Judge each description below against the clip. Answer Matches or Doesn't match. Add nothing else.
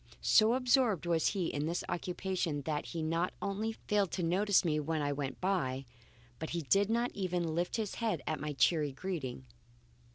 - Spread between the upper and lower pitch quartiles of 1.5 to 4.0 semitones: Doesn't match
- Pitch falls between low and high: Matches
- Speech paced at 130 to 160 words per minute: Doesn't match